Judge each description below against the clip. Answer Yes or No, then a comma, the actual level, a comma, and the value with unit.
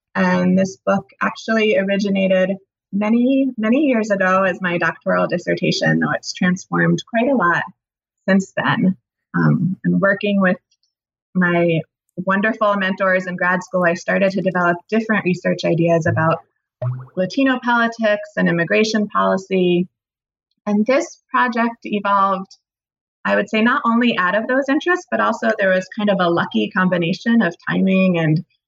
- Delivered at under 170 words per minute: Yes, average, 145 wpm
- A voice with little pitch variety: No, average, 3.7 semitones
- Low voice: No, high, 190 Hz